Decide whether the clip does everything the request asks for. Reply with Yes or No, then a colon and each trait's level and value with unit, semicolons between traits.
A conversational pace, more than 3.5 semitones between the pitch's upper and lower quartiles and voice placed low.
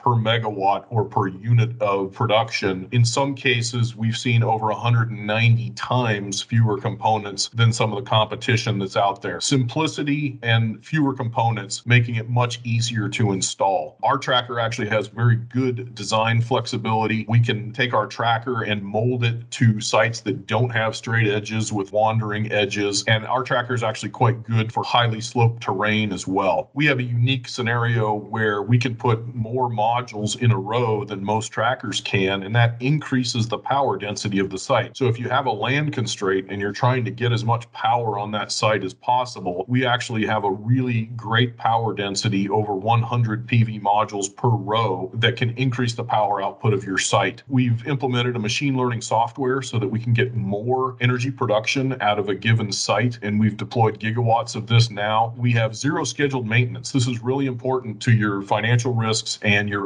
No: average, 185 wpm; average, 2.7 semitones; low, 115 Hz